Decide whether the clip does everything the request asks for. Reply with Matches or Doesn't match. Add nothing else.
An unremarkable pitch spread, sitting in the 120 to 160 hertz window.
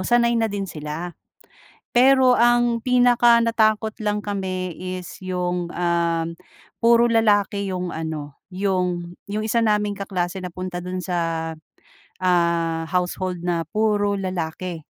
Doesn't match